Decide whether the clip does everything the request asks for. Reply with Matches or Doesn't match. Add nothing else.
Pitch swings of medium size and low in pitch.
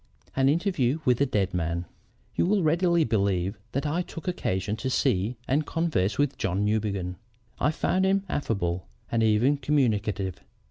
Doesn't match